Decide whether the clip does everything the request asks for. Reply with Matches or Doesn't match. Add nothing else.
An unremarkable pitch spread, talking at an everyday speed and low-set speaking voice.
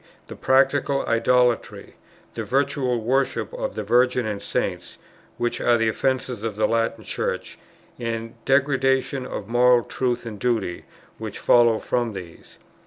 Doesn't match